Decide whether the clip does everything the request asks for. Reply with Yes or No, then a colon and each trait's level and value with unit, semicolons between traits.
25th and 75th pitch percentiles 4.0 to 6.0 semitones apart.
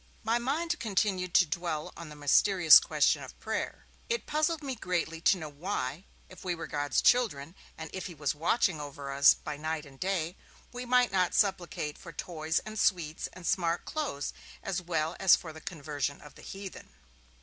Yes: average, 4.4 semitones